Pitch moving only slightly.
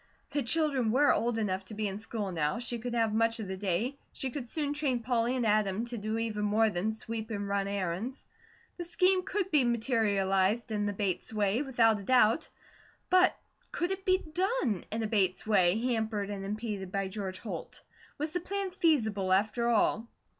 No: average, 4.1 semitones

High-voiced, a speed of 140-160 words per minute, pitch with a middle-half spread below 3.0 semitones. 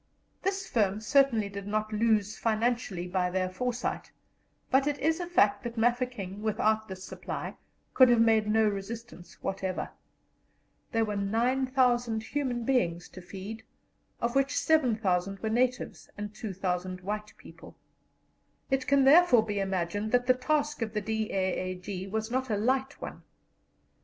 No: high, 220 Hz; average, 145 wpm; average, 4.2 semitones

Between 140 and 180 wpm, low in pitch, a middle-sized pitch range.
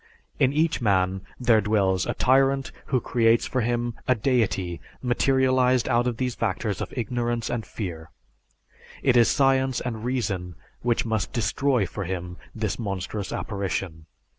Yes: average, 145 wpm; low, 115 Hz; average, 4.6 semitones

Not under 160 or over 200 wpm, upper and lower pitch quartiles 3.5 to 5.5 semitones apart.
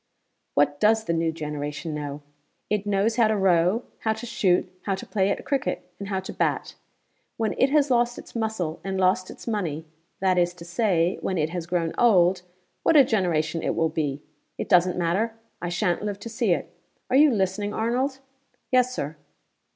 Yes: average, 190 wpm; average, 4.8 semitones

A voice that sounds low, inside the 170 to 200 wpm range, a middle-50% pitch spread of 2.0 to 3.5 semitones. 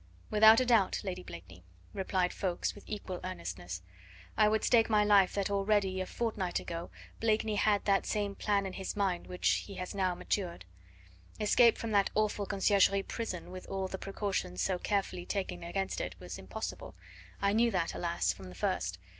No: high, 195 Hz; average, 180 wpm; average, 2.8 semitones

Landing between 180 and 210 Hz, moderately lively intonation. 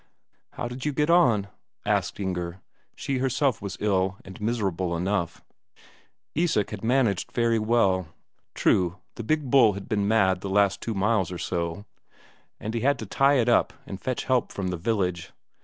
No: low, 105 Hz; average, 4.4 semitones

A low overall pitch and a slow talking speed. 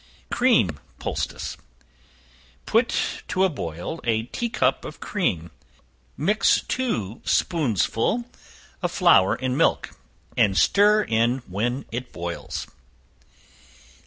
Yes: low, 125 Hz; slow, 100 wpm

